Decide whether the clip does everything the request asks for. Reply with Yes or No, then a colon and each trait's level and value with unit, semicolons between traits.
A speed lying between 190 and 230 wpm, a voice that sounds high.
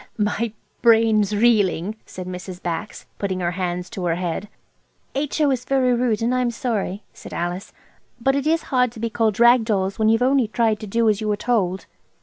Yes: average, 200 wpm; high, 220 Hz